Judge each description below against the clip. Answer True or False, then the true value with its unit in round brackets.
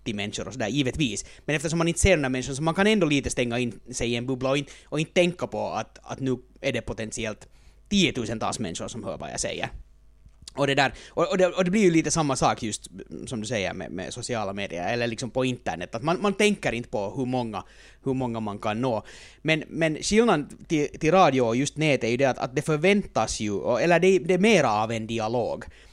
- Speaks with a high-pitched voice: False (130 Hz)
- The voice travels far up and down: True (5.7 semitones)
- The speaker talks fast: True (240 wpm)